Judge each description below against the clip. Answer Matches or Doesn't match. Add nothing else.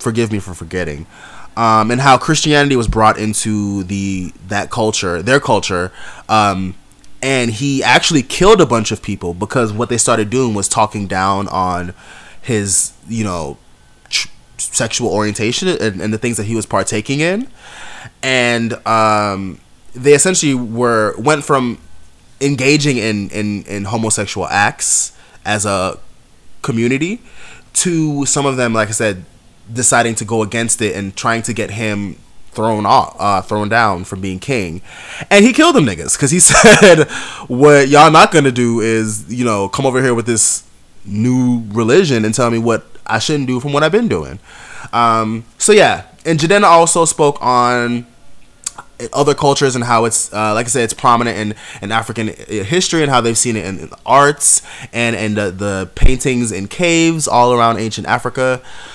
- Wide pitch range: Doesn't match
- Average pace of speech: Matches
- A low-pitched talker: Matches